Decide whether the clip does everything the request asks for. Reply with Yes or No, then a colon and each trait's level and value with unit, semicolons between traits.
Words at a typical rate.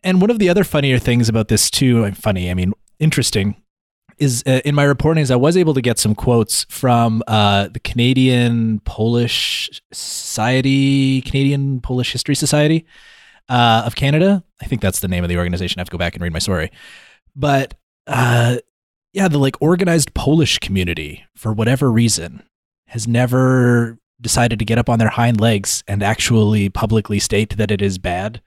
Yes: average, 180 wpm